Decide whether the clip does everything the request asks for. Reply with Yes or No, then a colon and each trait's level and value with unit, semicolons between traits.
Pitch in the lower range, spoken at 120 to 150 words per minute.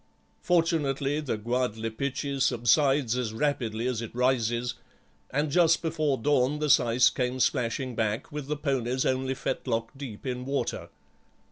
Yes: low, 130 Hz; slow, 135 wpm